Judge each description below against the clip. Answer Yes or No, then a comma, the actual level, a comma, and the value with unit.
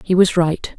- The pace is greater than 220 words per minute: Yes, fast, 230 wpm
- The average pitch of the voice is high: No, medium, 175 Hz